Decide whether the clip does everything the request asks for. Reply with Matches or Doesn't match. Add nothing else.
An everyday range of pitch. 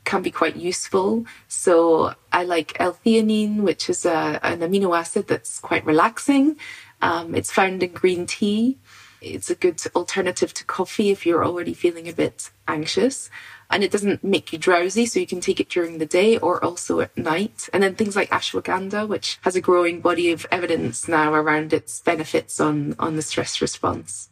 Matches